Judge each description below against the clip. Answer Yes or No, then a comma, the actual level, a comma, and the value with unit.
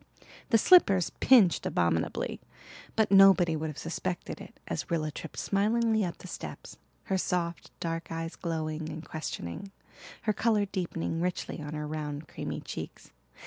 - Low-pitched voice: No, medium, 170 Hz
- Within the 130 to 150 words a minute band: Yes, average, 145 wpm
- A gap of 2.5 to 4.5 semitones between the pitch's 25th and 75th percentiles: Yes, average, 3.9 semitones